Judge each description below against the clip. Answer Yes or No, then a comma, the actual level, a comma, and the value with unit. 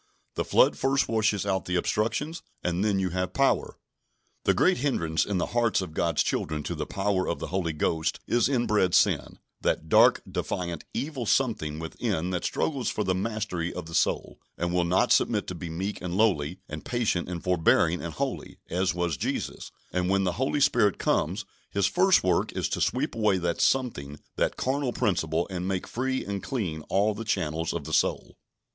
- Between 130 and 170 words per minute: No, average, 190 wpm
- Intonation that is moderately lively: Yes, average, 4.5 semitones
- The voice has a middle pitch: No, very low, 95 Hz